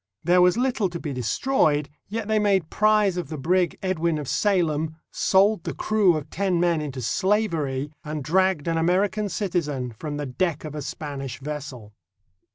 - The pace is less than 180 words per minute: Yes, average, 170 wpm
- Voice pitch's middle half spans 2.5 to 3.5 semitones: No, average, 4.5 semitones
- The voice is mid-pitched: Yes, medium, 170 Hz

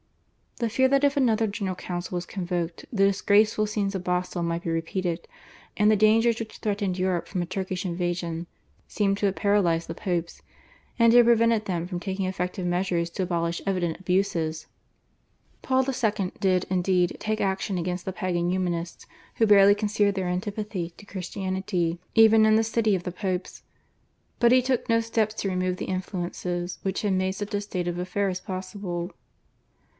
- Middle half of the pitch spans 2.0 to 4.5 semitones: Yes, average, 2.9 semitones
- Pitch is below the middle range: No, high, 190 Hz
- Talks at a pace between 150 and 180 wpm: Yes, average, 175 wpm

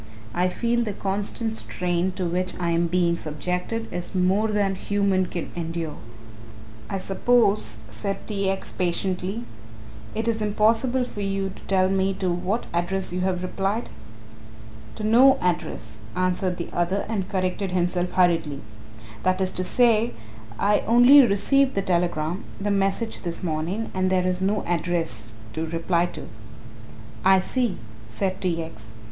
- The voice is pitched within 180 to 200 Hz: Yes, medium, 185 Hz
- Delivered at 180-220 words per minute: No, average, 150 wpm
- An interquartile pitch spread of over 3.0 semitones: No, average, 2.7 semitones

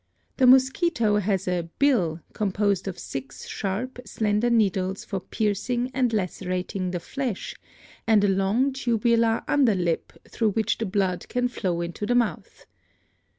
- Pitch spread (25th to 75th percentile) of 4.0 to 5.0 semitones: Yes, average, 4.4 semitones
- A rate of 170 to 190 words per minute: No, average, 145 wpm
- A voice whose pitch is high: Yes, high, 210 Hz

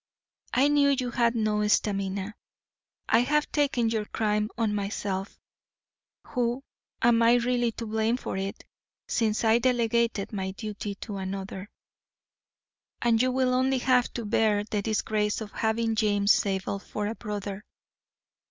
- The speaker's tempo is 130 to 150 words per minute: Yes, average, 140 wpm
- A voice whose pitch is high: Yes, high, 220 Hz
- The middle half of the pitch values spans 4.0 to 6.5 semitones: No, average, 2.7 semitones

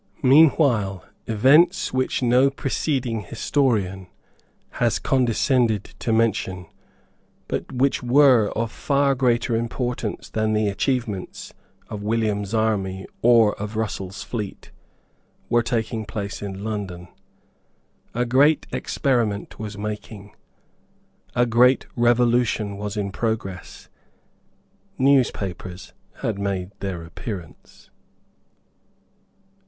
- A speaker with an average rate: No, slow, 95 wpm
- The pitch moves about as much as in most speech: Yes, average, 3.5 semitones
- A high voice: No, low, 110 Hz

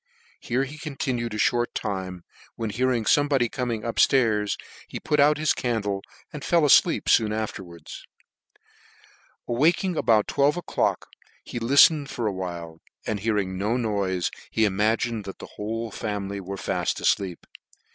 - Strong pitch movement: No, average, 4.5 semitones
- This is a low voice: Yes, low, 115 Hz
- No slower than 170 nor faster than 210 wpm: No, average, 145 wpm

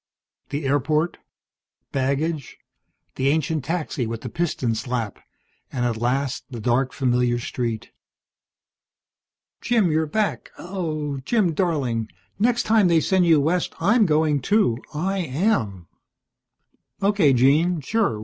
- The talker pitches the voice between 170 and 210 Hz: No, medium, 150 Hz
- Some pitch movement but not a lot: No, wide, 5.9 semitones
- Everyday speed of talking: No, slow, 120 wpm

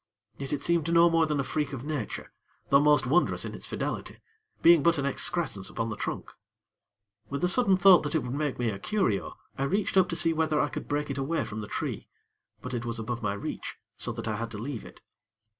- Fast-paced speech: Yes, fast, 235 wpm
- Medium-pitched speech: Yes, medium, 145 Hz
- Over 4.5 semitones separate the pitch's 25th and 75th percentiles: Yes, wide, 5.4 semitones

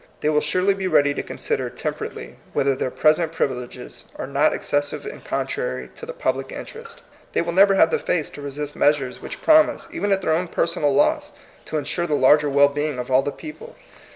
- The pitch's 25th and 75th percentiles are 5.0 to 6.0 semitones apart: Yes, average, 5.3 semitones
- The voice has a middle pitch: Yes, medium, 155 Hz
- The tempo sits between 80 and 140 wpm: No, fast, 205 wpm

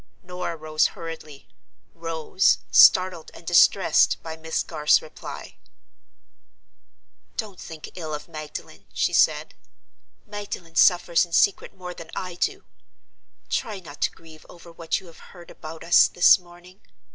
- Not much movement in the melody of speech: Yes, narrow, 2.1 semitones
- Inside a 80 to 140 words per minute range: Yes, slow, 135 wpm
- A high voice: No, medium, 170 Hz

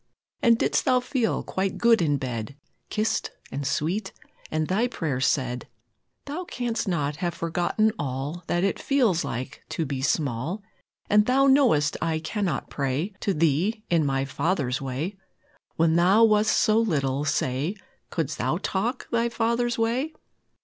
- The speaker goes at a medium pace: Yes, average, 150 wpm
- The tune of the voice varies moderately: No, wide, 7.8 semitones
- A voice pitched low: No, medium, 175 Hz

